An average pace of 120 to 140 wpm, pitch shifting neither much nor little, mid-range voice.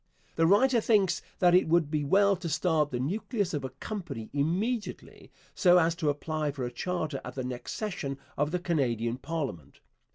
No: average, 185 wpm; average, 4.8 semitones; medium, 160 Hz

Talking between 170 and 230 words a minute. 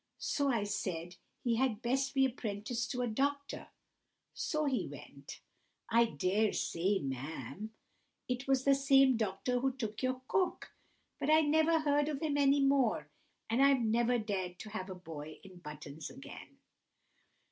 No: average, 150 wpm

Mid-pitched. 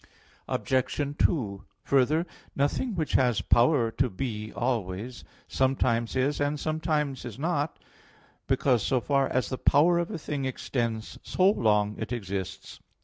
No: low, 130 Hz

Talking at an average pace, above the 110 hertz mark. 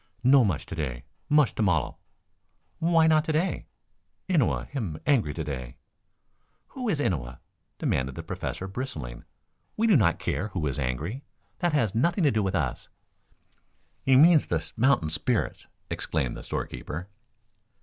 No: average, 155 wpm; low, 105 Hz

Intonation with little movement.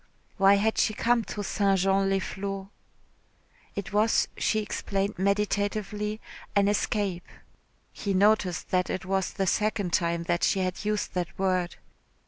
Yes: narrow, 1.9 semitones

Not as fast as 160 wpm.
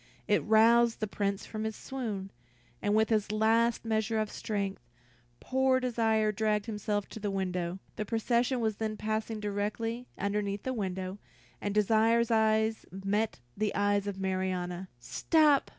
Yes: average, 150 wpm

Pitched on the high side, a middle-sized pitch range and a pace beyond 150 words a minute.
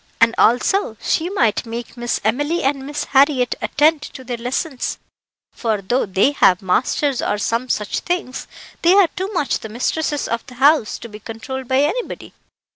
Yes: very high, 255 Hz; average, 4.3 semitones; average, 175 wpm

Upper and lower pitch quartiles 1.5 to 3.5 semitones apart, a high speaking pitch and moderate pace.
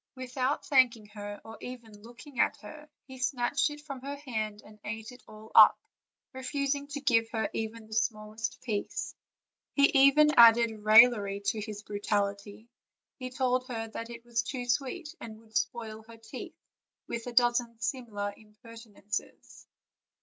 Yes: average, 2.9 semitones; high, 230 Hz; average, 155 wpm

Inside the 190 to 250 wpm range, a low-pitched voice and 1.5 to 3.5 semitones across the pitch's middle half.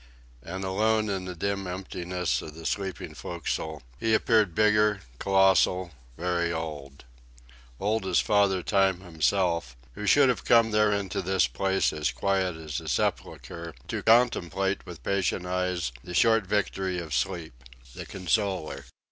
No: average, 145 wpm; very low, 95 Hz; average, 3.1 semitones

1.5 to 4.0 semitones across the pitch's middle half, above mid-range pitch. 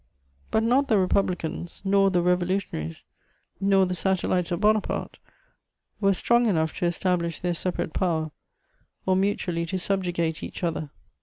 No: narrow, 2.5 semitones; medium, 180 Hz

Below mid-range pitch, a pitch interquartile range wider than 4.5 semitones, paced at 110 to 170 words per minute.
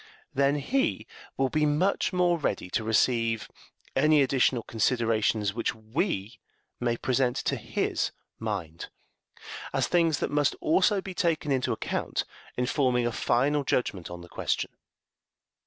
Yes: low, 130 Hz; average, 5.0 semitones; average, 140 wpm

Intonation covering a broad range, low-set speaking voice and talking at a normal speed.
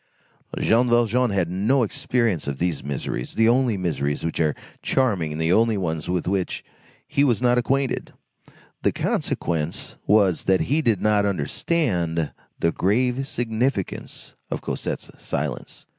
Yes: wide, 6.4 semitones; low, 100 Hz; average, 145 wpm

